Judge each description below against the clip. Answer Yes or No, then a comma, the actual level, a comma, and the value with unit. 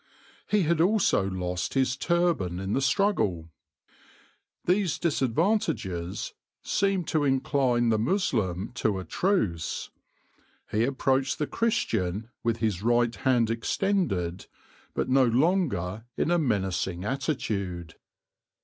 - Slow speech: Yes, slow, 115 wpm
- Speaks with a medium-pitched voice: No, low, 120 Hz